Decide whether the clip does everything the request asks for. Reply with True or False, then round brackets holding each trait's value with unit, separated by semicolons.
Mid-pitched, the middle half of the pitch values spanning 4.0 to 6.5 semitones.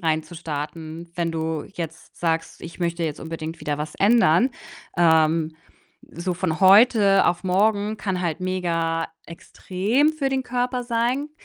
True (175 Hz; 4.3 semitones)